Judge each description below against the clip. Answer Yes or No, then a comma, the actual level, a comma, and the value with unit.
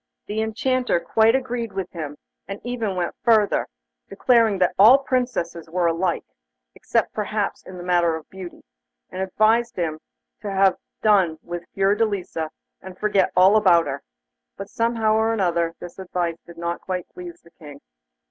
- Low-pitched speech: No, high, 190 Hz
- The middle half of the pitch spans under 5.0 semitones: Yes, average, 4.2 semitones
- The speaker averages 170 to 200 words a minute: No, average, 155 wpm